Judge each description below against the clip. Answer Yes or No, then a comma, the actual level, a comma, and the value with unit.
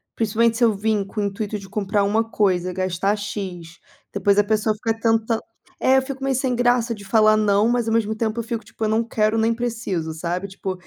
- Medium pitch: No, high, 215 Hz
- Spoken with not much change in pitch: Yes, narrow, 2.3 semitones